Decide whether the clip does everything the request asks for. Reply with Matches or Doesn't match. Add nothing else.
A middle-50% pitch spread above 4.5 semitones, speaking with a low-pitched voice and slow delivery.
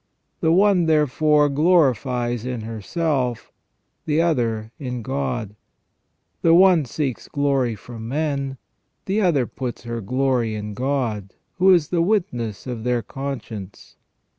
Matches